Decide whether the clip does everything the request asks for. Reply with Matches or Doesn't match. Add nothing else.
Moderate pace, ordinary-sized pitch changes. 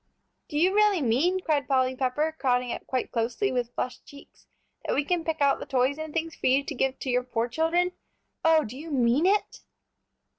Doesn't match